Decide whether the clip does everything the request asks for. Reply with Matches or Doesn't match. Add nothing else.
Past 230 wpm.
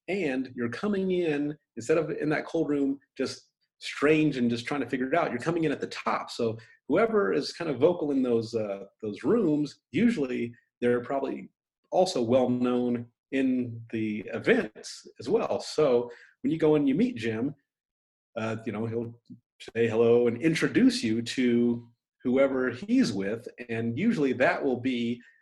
Doesn't match